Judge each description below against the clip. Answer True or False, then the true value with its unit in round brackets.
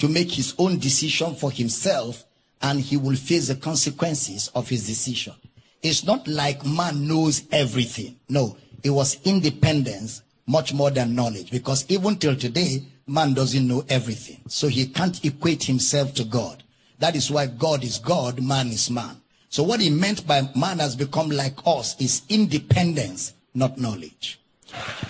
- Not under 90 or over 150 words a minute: False (165 wpm)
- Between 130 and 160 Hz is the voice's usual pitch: True (140 Hz)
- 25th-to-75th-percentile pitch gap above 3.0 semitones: True (3.6 semitones)